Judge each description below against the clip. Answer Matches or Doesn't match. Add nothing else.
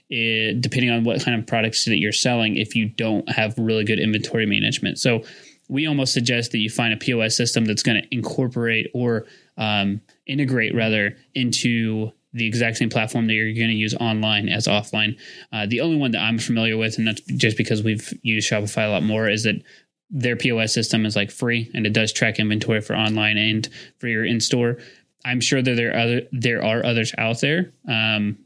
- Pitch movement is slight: Matches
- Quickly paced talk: Matches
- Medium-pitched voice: Doesn't match